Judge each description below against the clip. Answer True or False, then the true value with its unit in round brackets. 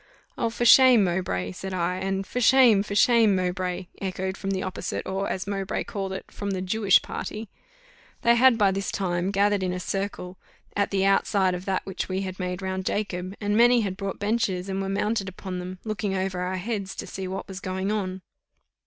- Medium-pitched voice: False (195 Hz)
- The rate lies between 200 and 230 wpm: True (205 wpm)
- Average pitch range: False (1.7 semitones)